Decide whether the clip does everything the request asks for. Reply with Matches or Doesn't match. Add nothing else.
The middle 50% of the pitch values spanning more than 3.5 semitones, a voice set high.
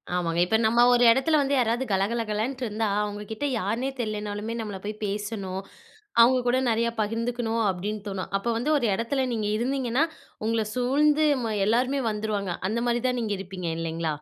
Doesn't match